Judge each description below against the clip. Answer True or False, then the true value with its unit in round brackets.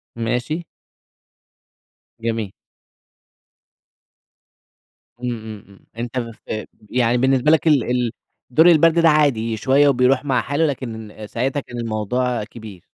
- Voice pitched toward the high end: False (125 Hz)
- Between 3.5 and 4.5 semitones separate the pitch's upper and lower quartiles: True (3.8 semitones)